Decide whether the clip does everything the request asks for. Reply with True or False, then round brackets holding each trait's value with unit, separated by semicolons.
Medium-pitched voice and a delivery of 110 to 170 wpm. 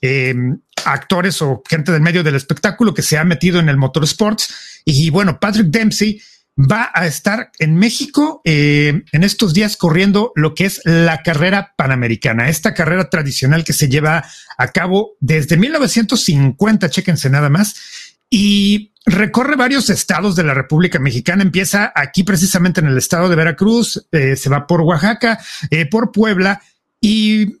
True (180 Hz; 160 wpm)